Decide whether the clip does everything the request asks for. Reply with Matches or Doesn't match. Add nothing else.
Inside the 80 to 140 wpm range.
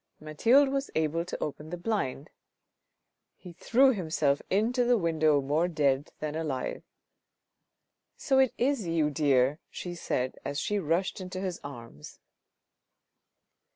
Matches